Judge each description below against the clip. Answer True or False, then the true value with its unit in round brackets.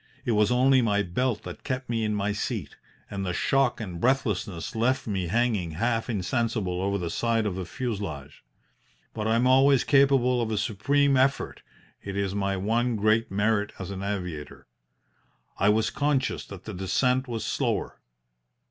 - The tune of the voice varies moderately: True (4.1 semitones)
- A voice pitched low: True (110 Hz)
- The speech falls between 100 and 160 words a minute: False (170 wpm)